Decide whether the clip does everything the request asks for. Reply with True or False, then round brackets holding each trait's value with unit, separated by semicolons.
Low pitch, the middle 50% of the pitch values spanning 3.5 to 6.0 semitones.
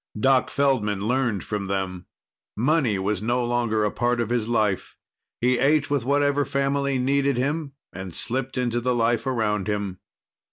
True (120 Hz; 4.4 semitones)